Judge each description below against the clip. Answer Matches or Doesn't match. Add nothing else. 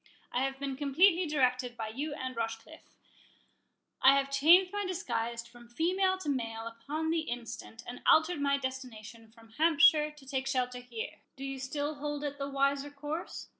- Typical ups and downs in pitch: Matches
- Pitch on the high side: Matches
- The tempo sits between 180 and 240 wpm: Doesn't match